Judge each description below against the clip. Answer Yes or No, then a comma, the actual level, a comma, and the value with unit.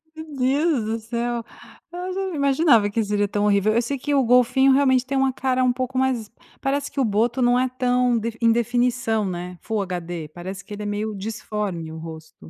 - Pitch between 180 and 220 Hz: No, high, 235 Hz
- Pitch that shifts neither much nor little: Yes, average, 4.1 semitones